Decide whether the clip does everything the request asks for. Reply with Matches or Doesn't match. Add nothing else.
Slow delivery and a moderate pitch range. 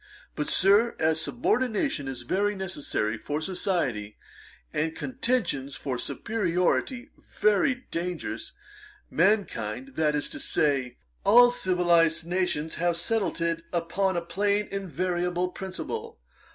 Matches